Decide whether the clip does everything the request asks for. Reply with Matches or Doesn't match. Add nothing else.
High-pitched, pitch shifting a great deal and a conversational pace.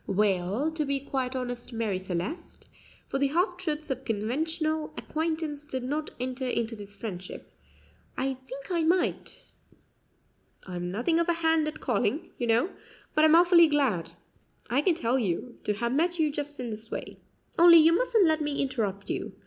Matches